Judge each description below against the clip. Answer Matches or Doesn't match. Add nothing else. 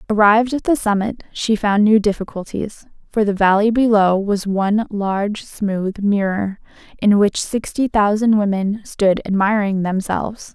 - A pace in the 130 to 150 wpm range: Matches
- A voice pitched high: Matches